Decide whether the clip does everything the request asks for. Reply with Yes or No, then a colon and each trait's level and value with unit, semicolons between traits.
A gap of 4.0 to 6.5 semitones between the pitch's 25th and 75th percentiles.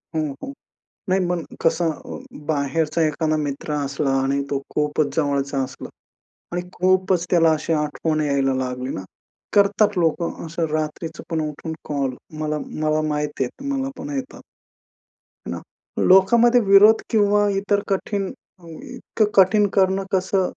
Yes: average, 4.7 semitones